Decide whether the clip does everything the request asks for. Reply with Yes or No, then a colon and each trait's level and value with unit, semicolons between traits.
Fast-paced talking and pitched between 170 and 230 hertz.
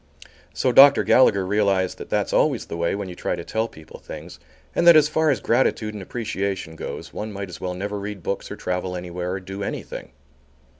No: fast, 210 wpm; low, 100 Hz